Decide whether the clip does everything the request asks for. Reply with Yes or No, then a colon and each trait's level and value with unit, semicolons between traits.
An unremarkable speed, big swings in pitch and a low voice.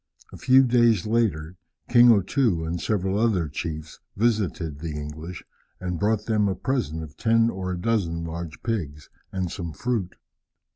Yes: average, 160 wpm; wide, 5.7 semitones; very low, 95 Hz